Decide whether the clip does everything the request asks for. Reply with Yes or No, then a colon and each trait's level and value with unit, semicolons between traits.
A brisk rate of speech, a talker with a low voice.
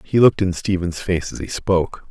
Yes: fast, 230 wpm; very low, 90 Hz